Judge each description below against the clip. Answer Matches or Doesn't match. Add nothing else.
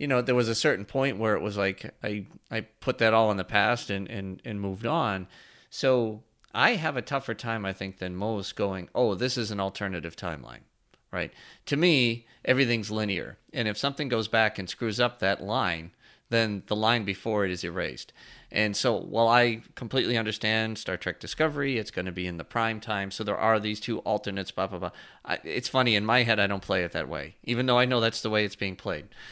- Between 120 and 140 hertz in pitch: Doesn't match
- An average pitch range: Matches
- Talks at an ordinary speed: Doesn't match